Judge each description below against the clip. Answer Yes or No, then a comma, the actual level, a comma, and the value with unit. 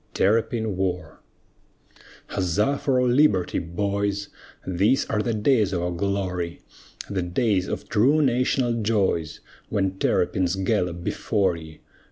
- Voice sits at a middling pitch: No, low, 100 Hz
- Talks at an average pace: No, slow, 125 wpm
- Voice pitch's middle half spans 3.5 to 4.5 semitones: Yes, average, 4.1 semitones